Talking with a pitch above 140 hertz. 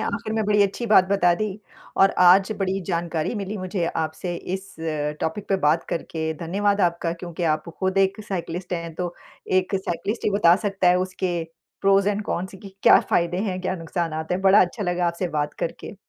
Yes: medium, 185 Hz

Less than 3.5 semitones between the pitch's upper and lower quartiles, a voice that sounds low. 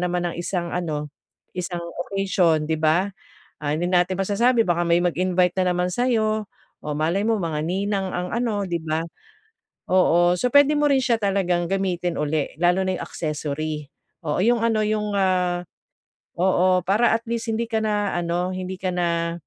No: average, 3.1 semitones; medium, 180 Hz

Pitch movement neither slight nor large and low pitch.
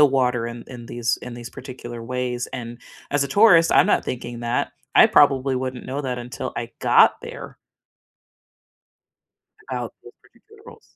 No: narrow, 2.2 semitones; low, 125 Hz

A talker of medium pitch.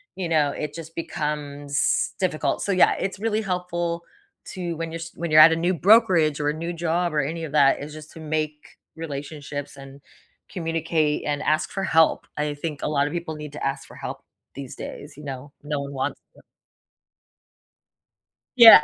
Yes: medium, 155 Hz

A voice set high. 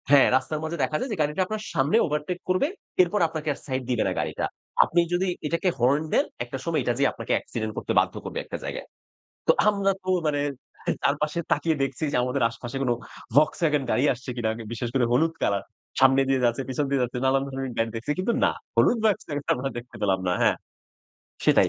No: medium, 140 Hz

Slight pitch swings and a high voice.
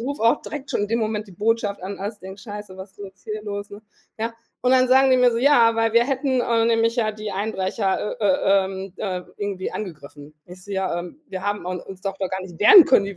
No: average, 3.3 semitones; high, 205 Hz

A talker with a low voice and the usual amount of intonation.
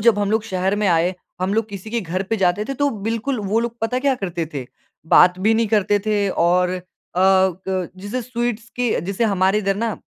No: high, 205 Hz; average, 3.4 semitones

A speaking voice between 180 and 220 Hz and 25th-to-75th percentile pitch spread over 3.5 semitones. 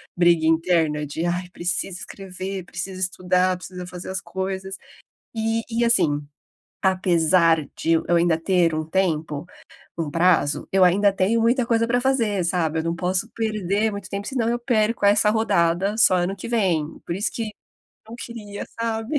Yes: medium, 185 Hz; average, 4.0 semitones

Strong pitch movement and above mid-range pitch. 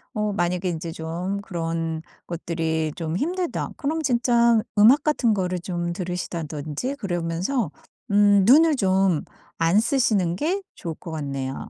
No: wide, 6.1 semitones; medium, 180 Hz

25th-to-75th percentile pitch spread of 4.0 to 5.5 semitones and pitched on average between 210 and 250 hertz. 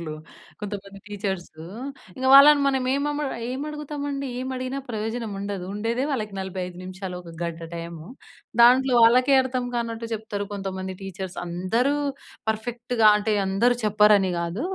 Yes: average, 5.0 semitones; high, 215 Hz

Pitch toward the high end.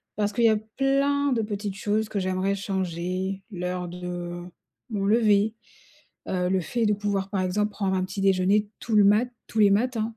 Yes: high, 200 Hz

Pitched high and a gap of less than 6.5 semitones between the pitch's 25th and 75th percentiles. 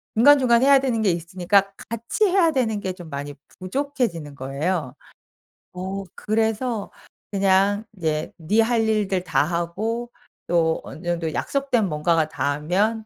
Yes: high, 195 Hz; average, 5.3 semitones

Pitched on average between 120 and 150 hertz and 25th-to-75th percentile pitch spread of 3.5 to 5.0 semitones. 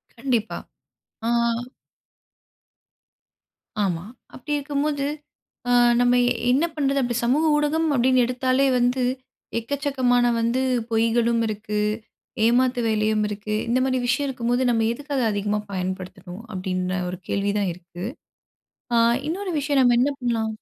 No: high, 240 Hz; average, 3.9 semitones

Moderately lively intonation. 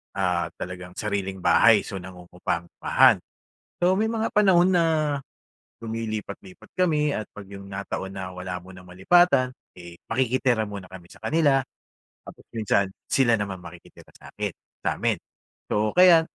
No: wide, 6.7 semitones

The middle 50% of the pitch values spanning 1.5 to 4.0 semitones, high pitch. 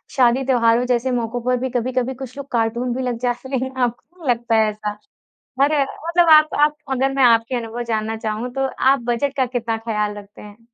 Yes: narrow, 2.5 semitones; high, 245 Hz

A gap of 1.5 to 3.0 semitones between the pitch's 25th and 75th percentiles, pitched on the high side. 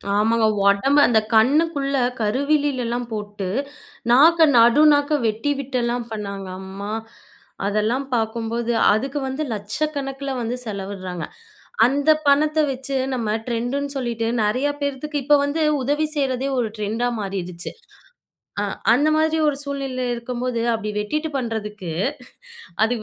No: average, 4.7 semitones; high, 245 Hz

